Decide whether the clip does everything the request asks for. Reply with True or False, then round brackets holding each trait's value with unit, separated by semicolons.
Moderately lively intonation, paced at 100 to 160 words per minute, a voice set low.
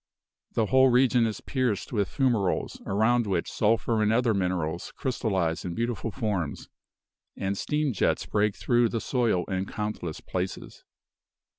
True (4.1 semitones; 140 wpm; 110 Hz)